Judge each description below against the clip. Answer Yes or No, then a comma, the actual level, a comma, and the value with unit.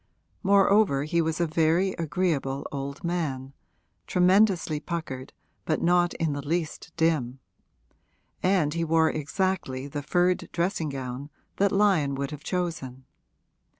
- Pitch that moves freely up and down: No, average, 4.2 semitones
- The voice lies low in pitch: No, medium, 160 Hz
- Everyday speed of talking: No, slow, 125 wpm